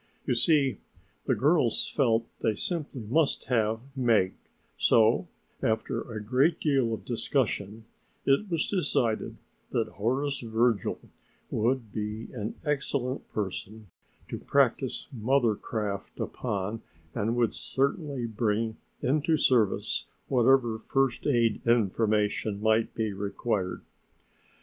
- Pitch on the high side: No, low, 115 Hz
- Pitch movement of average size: Yes, average, 3.7 semitones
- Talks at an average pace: No, slow, 110 wpm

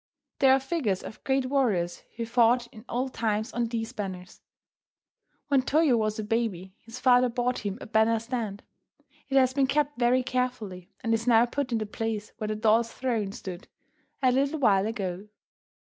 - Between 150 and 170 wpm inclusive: No, average, 180 wpm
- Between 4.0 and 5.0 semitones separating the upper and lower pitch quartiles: No, average, 3.1 semitones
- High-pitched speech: Yes, high, 230 Hz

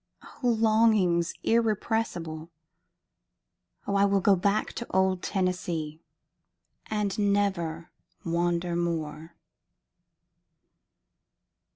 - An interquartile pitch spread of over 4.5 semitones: No, average, 3.5 semitones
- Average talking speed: No, slow, 75 wpm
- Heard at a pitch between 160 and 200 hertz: Yes, medium, 185 Hz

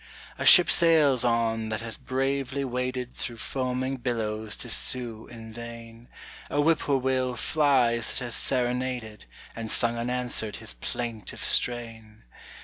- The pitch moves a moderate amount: No, narrow, 2.2 semitones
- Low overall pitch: Yes, low, 120 Hz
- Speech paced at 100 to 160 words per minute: Yes, average, 140 wpm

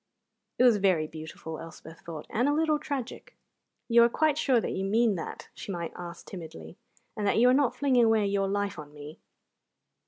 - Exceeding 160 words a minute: Yes, average, 195 wpm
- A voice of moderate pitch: No, high, 205 Hz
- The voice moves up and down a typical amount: No, wide, 7.0 semitones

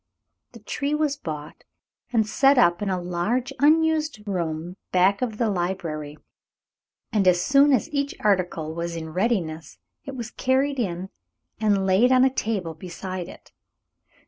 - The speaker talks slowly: No, average, 150 wpm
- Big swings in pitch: Yes, wide, 6.9 semitones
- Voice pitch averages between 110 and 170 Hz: No, high, 200 Hz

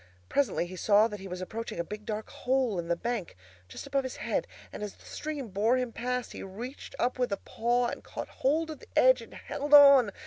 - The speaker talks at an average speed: No, fast, 235 wpm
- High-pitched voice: Yes, high, 235 Hz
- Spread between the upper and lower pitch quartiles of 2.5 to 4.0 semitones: No, average, 4.6 semitones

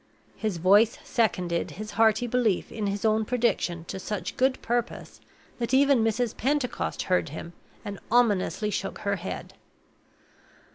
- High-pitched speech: Yes, high, 215 Hz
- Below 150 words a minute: Yes, average, 140 wpm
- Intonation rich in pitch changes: No, average, 3.9 semitones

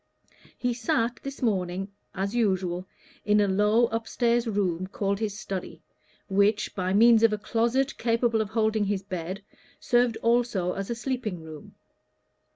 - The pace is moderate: Yes, average, 155 wpm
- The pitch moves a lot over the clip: No, average, 3.3 semitones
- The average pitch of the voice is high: Yes, high, 210 Hz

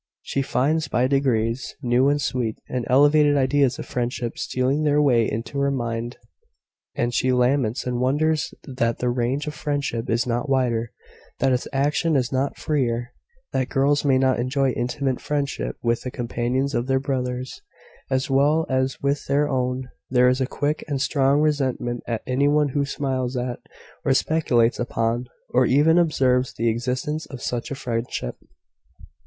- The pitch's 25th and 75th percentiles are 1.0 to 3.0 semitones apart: Yes, narrow, 2.6 semitones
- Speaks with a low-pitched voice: Yes, low, 130 Hz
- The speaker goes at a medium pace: Yes, average, 165 wpm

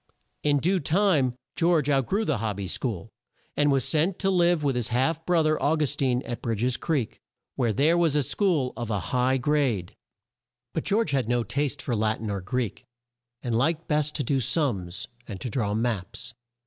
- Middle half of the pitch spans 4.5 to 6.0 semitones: Yes, average, 5.0 semitones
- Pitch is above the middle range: No, low, 135 Hz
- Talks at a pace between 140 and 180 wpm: No, average, 200 wpm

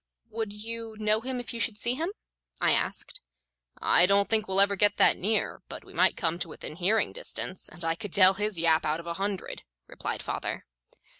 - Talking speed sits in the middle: No, fast, 210 wpm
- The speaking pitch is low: No, high, 205 Hz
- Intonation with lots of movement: No, average, 3.8 semitones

